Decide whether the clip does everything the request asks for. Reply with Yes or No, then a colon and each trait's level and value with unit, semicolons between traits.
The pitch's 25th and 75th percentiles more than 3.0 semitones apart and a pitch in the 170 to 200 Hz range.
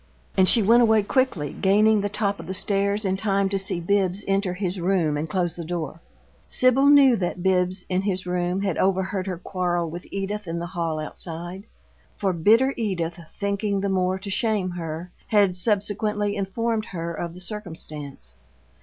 No: average, 2.7 semitones; high, 190 Hz